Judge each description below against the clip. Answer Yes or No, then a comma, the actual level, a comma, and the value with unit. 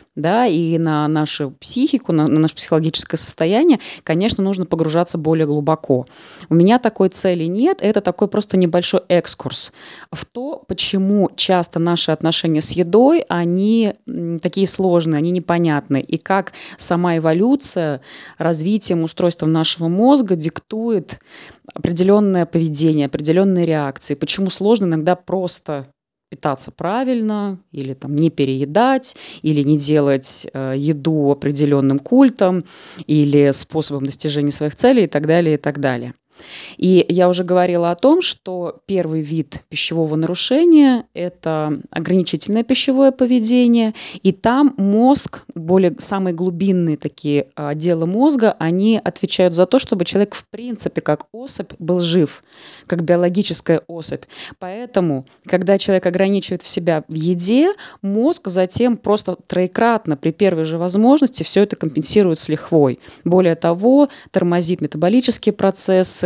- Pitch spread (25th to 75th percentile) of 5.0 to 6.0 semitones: No, average, 4.3 semitones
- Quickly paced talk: No, average, 130 wpm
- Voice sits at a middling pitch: Yes, medium, 175 Hz